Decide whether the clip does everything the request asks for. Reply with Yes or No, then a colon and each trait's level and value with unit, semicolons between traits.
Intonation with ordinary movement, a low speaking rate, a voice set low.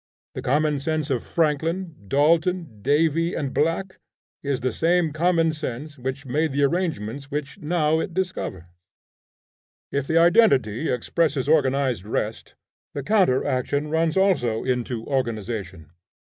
No: average, 4.3 semitones; slow, 130 wpm; medium, 145 Hz